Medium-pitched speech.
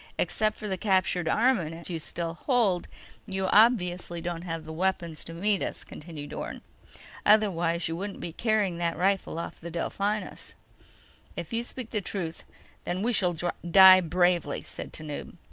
Yes: medium, 180 Hz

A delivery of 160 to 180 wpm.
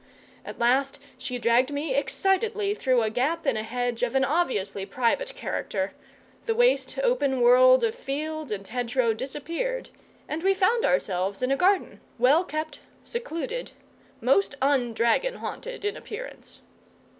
No: average, 150 wpm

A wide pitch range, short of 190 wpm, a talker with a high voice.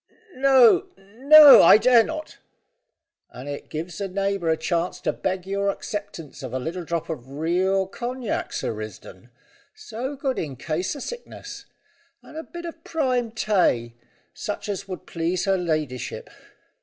Yes: wide, 7.6 semitones; average, 155 wpm; high, 195 Hz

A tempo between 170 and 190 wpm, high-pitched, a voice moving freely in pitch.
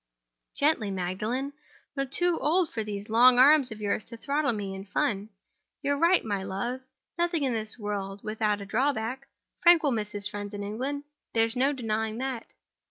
No: average, 180 wpm; high, 225 Hz; average, 5.0 semitones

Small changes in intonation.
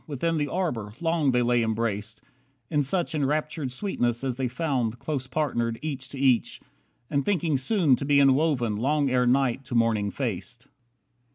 No: average, 4.1 semitones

